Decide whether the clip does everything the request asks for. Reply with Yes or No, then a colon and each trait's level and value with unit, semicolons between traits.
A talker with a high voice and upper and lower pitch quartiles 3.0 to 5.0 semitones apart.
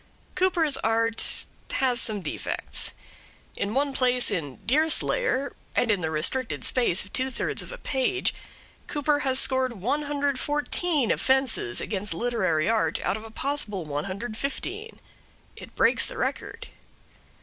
No: very high, 255 Hz; wide, 5.4 semitones